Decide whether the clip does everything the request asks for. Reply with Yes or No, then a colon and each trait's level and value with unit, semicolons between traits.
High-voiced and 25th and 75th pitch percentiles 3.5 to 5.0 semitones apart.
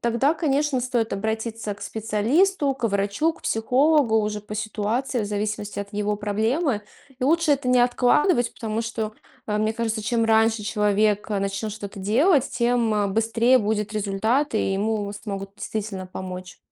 No: high, 220 Hz; average, 3.0 semitones